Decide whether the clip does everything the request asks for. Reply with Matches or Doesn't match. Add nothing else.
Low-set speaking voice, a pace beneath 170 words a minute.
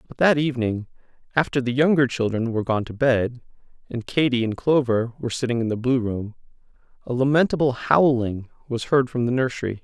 Doesn't match